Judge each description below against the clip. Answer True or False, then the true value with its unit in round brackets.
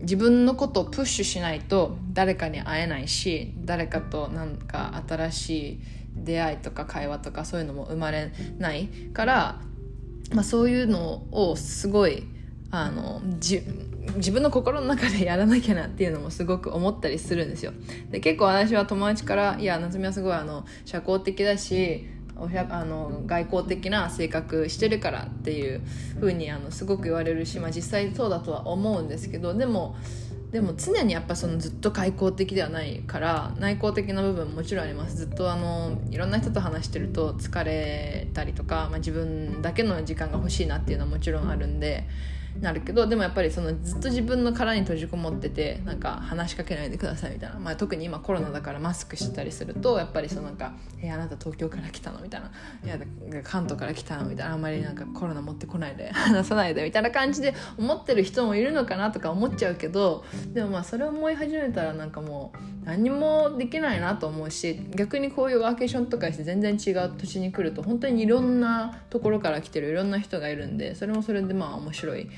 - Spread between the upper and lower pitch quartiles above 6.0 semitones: False (5.7 semitones)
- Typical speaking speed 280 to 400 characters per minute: False (415 characters per minute)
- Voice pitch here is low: False (175 Hz)